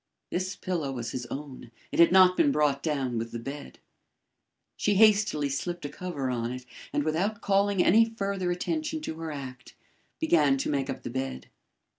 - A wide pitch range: Yes, wide, 6.3 semitones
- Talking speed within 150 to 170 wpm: No, average, 180 wpm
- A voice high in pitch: No, medium, 155 Hz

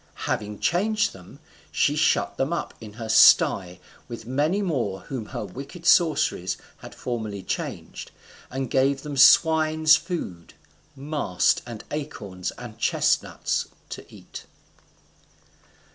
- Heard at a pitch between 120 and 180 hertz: Yes, low, 135 Hz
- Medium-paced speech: No, slow, 120 wpm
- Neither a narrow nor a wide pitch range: No, wide, 6.6 semitones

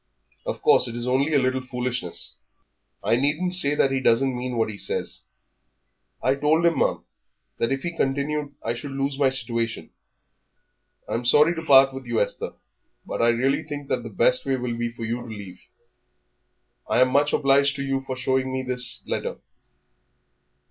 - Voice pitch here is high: No, low, 130 Hz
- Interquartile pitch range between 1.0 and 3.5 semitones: Yes, average, 2.7 semitones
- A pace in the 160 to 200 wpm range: Yes, average, 185 wpm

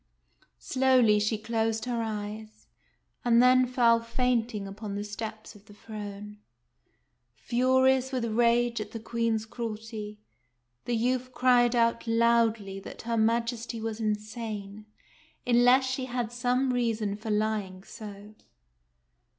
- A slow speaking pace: Yes, slow, 125 wpm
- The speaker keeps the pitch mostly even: Yes, narrow, 2.2 semitones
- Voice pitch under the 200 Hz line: No, high, 230 Hz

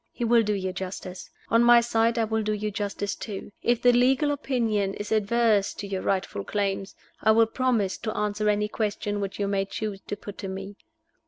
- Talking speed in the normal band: No, fast, 210 wpm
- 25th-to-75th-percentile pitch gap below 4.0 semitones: Yes, narrow, 2.5 semitones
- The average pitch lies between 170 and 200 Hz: No, high, 210 Hz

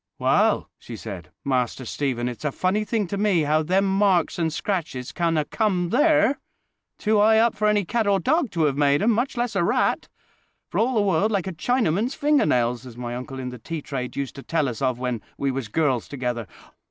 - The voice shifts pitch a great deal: Yes, wide, 8.1 semitones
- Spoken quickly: Yes, fast, 215 wpm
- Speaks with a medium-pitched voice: Yes, medium, 165 Hz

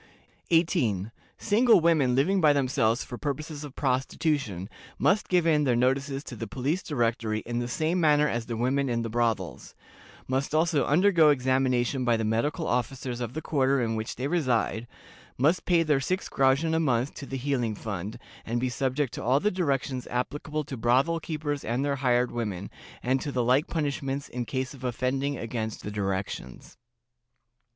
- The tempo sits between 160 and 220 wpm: Yes, average, 175 wpm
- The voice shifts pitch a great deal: No, average, 3.9 semitones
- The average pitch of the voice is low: Yes, low, 130 Hz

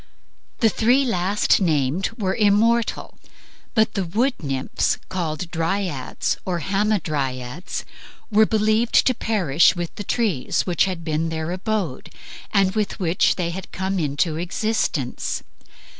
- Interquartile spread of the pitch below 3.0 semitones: No, average, 4.7 semitones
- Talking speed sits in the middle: No, slow, 130 wpm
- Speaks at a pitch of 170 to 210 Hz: Yes, medium, 185 Hz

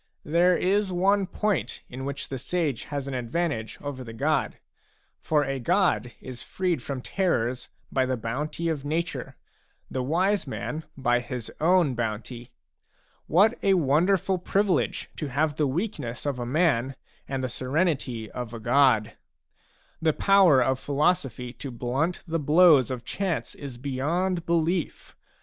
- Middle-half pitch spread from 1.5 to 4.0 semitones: No, wide, 5.5 semitones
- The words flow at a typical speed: Yes, average, 150 wpm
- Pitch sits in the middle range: Yes, medium, 145 Hz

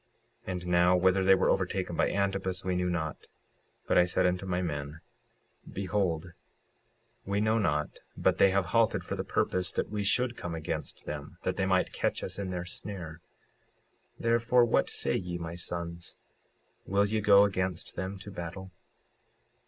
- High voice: No, very low, 90 Hz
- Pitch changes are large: No, narrow, 2.4 semitones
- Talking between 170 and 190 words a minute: Yes, average, 175 wpm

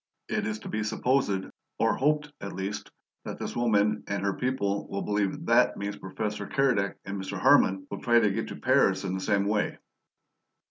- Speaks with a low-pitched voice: Yes, low, 105 Hz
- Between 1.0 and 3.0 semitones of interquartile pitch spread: Yes, narrow, 2.4 semitones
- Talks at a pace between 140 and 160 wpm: No, average, 190 wpm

